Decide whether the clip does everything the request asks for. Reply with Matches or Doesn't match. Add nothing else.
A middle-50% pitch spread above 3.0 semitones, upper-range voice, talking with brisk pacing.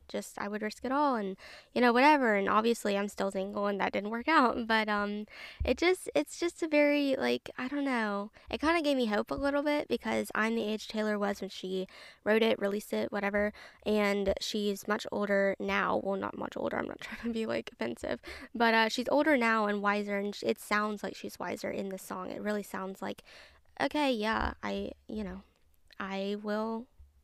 Matches